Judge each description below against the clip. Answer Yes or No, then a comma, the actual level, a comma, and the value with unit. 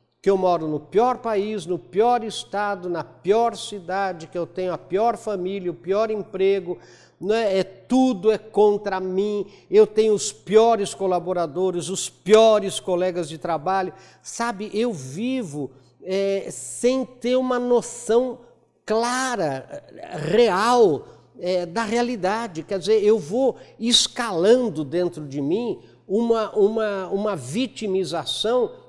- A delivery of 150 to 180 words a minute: No, average, 130 wpm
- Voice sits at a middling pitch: No, high, 200 Hz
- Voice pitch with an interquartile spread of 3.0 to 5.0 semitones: Yes, average, 4.1 semitones